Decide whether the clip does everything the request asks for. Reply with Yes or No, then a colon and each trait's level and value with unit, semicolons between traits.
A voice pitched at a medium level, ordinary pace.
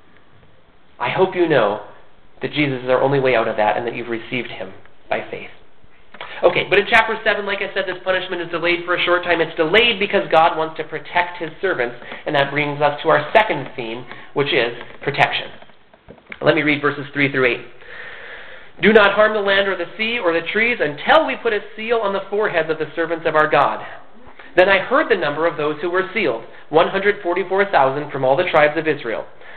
No: medium, 165 Hz; fast, 215 wpm